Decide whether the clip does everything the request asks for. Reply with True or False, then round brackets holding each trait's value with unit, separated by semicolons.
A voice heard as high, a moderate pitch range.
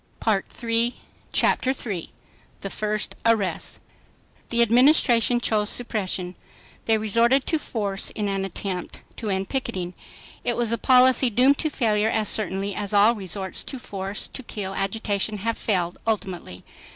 True (215 Hz; 3.3 semitones)